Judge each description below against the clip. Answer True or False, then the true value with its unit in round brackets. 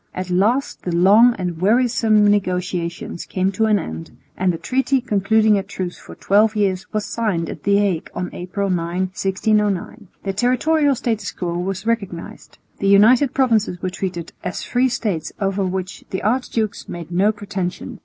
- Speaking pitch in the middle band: False (200 Hz)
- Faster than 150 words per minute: True (165 wpm)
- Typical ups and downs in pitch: True (3.3 semitones)